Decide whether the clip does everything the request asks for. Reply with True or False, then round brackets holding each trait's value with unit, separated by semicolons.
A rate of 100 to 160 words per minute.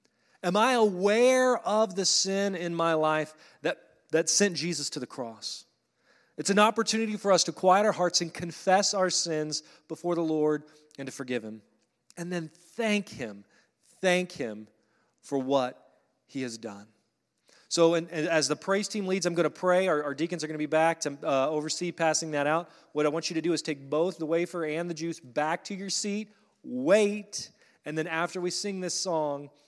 False (195 wpm)